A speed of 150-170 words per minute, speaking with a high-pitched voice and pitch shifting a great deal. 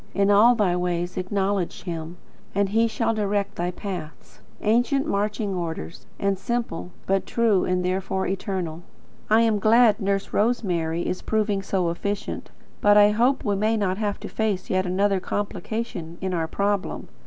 No: average, 160 wpm; high, 200 Hz; average, 2.7 semitones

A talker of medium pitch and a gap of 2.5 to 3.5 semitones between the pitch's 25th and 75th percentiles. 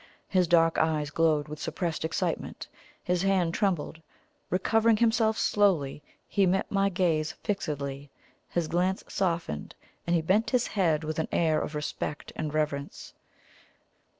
No: medium, 170 Hz; average, 3.9 semitones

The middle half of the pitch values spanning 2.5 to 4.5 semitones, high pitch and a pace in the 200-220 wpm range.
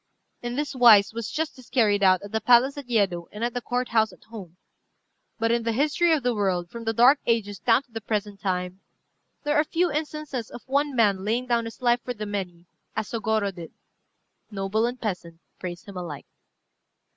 Yes: average, 3.8 semitones; high, 225 Hz; fast, 205 wpm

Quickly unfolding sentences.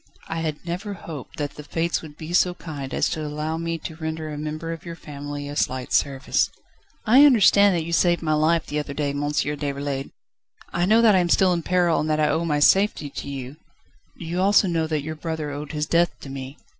Yes: fast, 235 wpm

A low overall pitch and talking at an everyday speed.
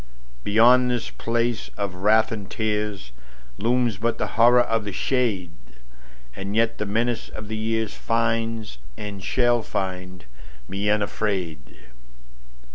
No: low, 105 Hz; slow, 115 wpm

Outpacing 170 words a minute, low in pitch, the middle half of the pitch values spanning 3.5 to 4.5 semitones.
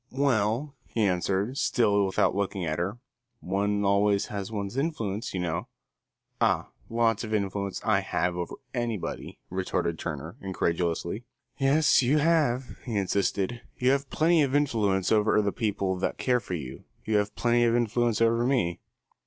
No: average, 155 wpm; low, 105 Hz; average, 4.0 semitones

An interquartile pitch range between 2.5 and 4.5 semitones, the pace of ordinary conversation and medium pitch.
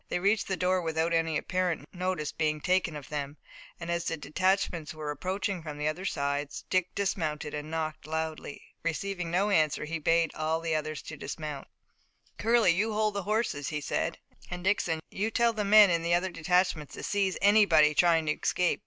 Yes: average, 3.4 semitones; average, 190 wpm; medium, 170 Hz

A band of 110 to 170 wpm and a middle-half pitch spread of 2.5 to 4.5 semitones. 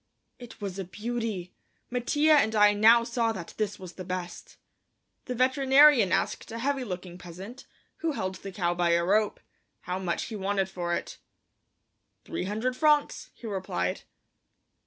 No: average, 155 wpm; average, 4.9 semitones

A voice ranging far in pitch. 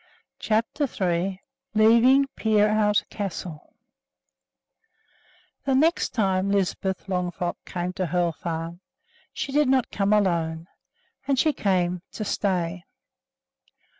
No: average, 3.7 semitones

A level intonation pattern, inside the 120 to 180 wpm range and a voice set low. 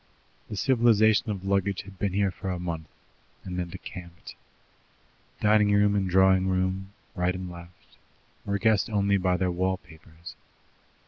Yes: narrow, 2.1 semitones; average, 150 wpm; very low, 95 Hz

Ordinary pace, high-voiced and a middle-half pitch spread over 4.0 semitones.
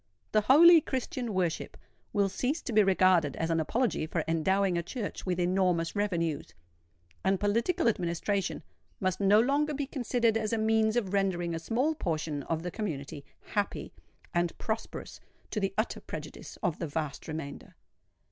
Yes: average, 160 wpm; high, 195 Hz; average, 5.1 semitones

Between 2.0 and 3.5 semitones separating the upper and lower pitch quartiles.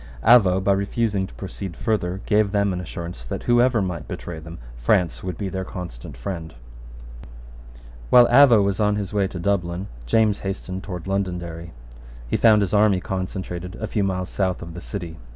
Yes: narrow, 2.6 semitones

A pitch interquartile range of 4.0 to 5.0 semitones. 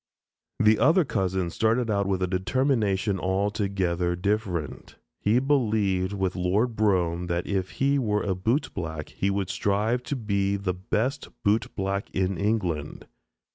No: average, 3.0 semitones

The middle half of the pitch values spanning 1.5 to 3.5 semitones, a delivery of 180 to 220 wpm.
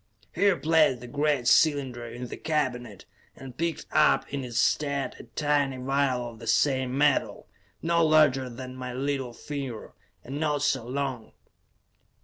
No: average, 2.9 semitones; average, 150 wpm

